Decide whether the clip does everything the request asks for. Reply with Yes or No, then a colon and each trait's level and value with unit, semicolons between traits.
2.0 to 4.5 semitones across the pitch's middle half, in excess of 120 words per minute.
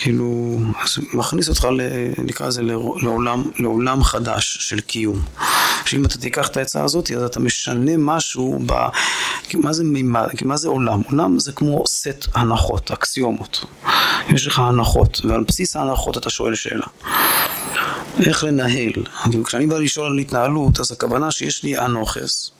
Yes: average, 3.8 semitones; fast, 150 wpm